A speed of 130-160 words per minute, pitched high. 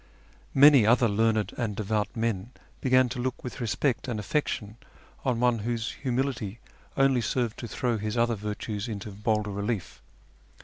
No: average, 150 wpm; low, 115 Hz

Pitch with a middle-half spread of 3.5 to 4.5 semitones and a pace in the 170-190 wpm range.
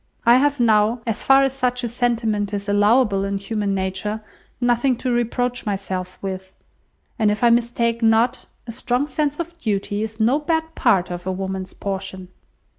Yes: average, 3.8 semitones; average, 175 wpm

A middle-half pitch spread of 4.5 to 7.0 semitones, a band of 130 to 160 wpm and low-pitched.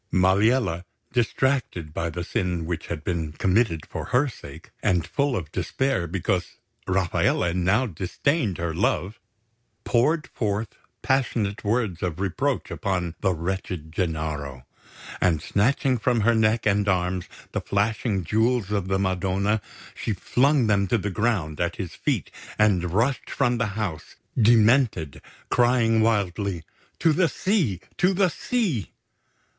Yes: average, 5.1 semitones; average, 140 wpm; low, 100 Hz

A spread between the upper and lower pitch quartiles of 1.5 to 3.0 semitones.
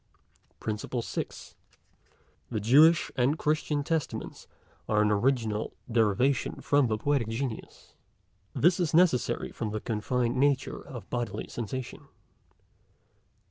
No: average, 4.6 semitones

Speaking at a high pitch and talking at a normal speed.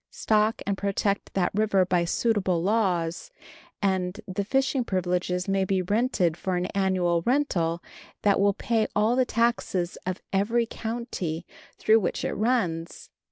Yes: high, 195 Hz; average, 145 wpm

